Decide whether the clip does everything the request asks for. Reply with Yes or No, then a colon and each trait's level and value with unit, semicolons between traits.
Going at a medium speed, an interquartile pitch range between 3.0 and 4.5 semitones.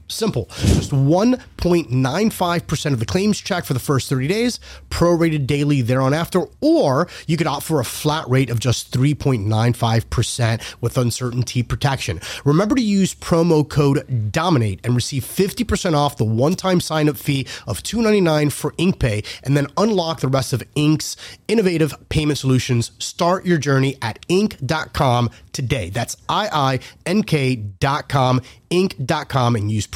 No: average, 150 wpm; wide, 5.5 semitones